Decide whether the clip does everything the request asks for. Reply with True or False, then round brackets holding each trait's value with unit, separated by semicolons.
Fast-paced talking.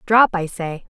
False (185 wpm)